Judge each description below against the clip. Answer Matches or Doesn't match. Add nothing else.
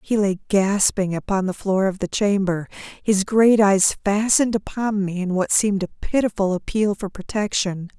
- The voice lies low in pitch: Doesn't match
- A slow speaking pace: Doesn't match